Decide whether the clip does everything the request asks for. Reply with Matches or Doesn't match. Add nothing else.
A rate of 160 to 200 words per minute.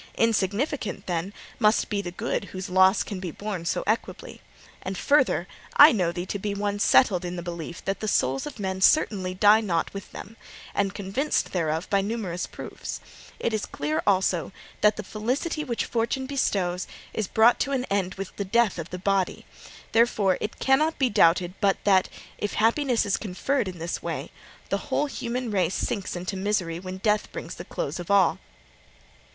Matches